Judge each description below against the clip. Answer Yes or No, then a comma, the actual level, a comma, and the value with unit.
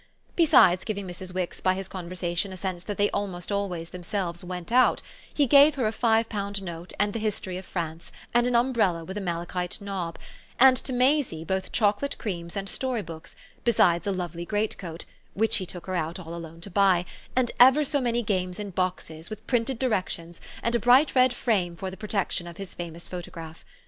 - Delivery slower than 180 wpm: No, average, 195 wpm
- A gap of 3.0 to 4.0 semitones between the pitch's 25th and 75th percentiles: No, average, 4.6 semitones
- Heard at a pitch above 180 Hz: Yes, high, 190 Hz